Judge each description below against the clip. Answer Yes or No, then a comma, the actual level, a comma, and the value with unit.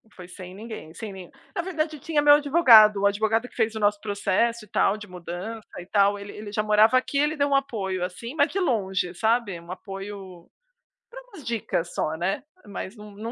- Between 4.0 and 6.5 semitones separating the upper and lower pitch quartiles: Yes, average, 4.4 semitones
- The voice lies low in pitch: No, high, 210 Hz